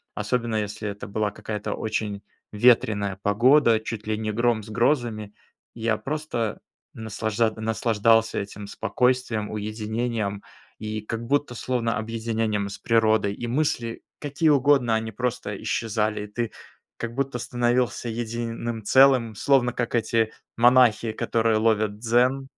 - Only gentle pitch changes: Yes, narrow, 2.1 semitones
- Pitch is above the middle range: No, low, 115 Hz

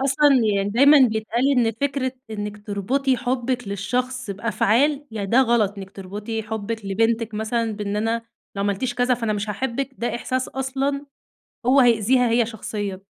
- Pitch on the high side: Yes, high, 230 Hz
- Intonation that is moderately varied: Yes, average, 3.7 semitones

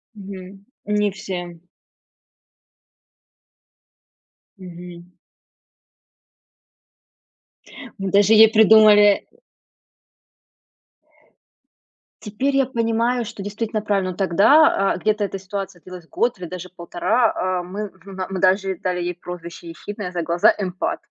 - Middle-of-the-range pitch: No, high, 195 Hz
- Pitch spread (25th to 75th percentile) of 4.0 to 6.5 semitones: No, average, 2.7 semitones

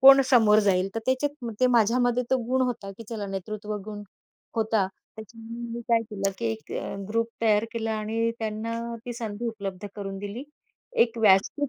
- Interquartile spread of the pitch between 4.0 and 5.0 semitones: No, narrow, 2.4 semitones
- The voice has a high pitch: Yes, high, 225 Hz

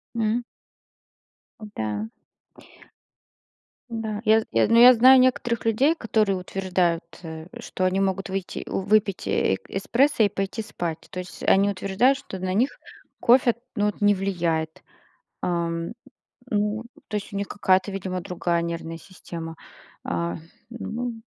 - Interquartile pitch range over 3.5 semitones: Yes, average, 4.0 semitones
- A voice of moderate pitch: No, high, 195 Hz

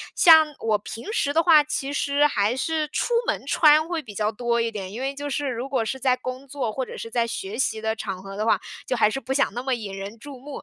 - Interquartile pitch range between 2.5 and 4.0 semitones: No, average, 4.7 semitones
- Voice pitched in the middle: No, very high, 255 Hz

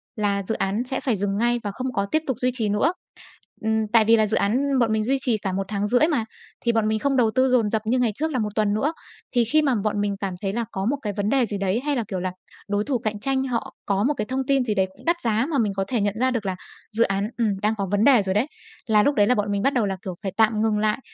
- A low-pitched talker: No, high, 220 Hz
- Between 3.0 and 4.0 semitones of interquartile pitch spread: Yes, average, 3.6 semitones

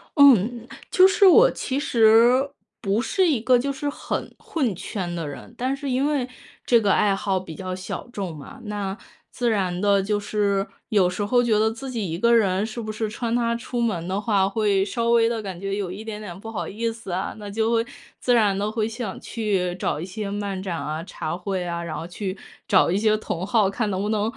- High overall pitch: Yes, high, 210 Hz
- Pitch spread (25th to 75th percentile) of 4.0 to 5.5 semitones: No, average, 3.4 semitones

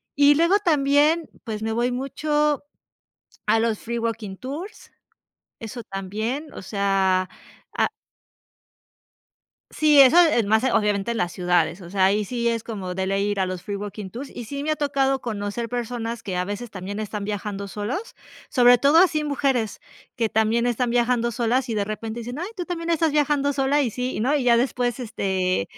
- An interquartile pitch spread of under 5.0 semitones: No, average, 5.3 semitones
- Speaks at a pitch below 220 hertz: No, high, 235 Hz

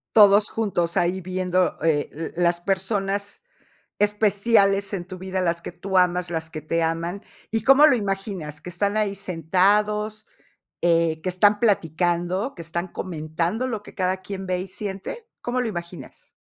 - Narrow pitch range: No, average, 3.1 semitones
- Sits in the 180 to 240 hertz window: Yes, medium, 185 Hz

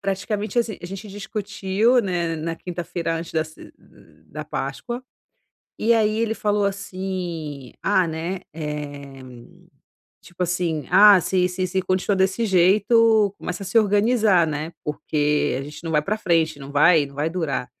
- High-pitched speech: No, medium, 180 Hz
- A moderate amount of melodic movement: Yes, average, 4.3 semitones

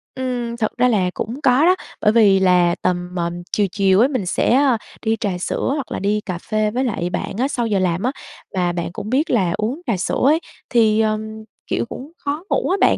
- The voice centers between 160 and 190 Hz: No, high, 215 Hz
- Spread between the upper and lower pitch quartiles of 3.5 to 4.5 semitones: No, average, 5.1 semitones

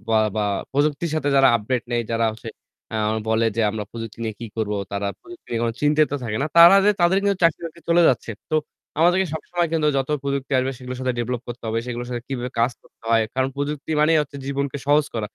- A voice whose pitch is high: No, low, 130 Hz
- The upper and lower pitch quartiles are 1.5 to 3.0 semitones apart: No, average, 4.8 semitones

